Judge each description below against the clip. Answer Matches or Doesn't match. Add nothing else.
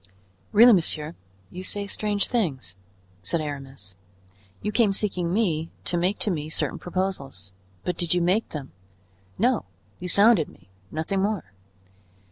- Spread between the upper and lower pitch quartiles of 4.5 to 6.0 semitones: Matches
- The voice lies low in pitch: Doesn't match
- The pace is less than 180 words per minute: Matches